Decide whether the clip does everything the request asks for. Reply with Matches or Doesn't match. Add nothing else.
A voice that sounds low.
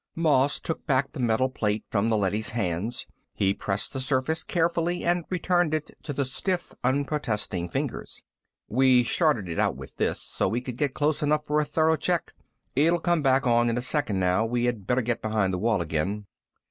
Matches